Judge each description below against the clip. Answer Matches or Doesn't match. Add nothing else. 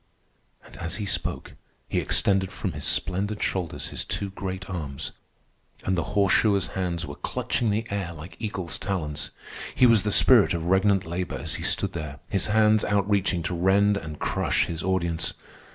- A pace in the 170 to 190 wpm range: Matches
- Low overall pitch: Matches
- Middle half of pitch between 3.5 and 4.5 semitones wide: Doesn't match